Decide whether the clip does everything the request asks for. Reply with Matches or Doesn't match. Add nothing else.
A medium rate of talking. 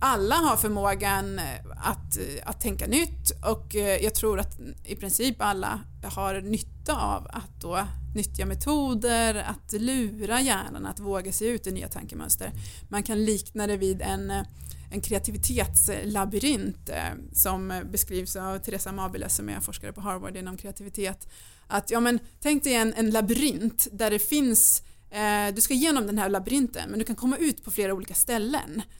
Matches